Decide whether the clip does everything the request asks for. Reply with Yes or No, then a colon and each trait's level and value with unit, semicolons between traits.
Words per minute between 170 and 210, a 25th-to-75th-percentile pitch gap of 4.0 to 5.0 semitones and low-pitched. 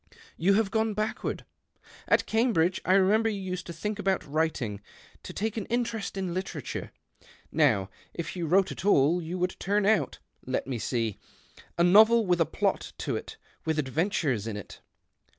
No: average, 185 wpm; average, 4.7 semitones; medium, 185 Hz